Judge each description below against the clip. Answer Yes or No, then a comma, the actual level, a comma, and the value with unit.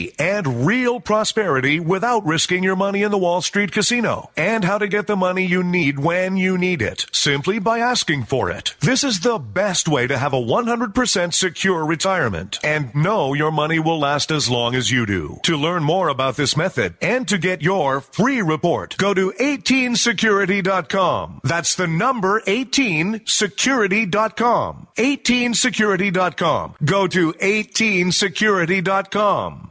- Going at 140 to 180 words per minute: Yes, average, 150 wpm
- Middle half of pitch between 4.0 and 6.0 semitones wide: Yes, average, 5.1 semitones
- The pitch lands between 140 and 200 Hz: Yes, high, 190 Hz